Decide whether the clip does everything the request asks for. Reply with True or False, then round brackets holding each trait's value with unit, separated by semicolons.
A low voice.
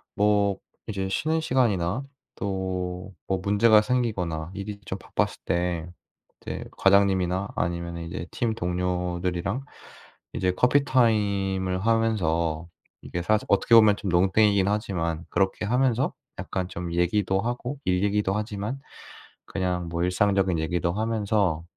True (95 Hz)